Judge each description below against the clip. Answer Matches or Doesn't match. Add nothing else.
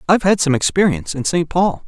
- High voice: Doesn't match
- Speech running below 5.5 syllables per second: Doesn't match